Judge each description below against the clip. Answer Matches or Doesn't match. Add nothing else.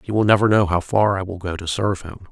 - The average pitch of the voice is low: Matches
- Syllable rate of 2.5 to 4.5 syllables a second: Doesn't match